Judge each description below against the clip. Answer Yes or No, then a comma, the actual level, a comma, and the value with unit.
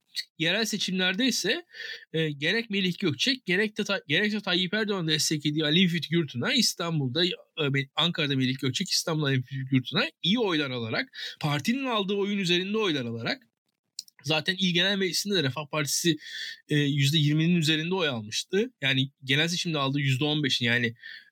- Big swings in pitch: Yes, wide, 5.9 semitones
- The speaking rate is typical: No, fast, 150 wpm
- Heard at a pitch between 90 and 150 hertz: No, medium, 165 Hz